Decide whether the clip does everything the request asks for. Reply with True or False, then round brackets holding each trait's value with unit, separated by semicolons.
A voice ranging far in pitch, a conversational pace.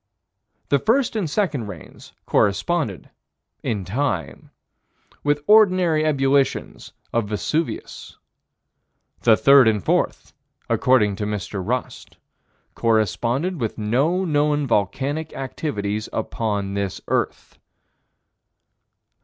False (6.4 semitones; 95 wpm)